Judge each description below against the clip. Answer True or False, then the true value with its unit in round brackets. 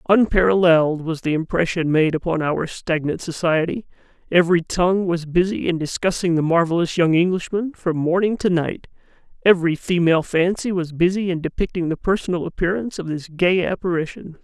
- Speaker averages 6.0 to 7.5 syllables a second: False (5.6 syllables/s)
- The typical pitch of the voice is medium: True (170 Hz)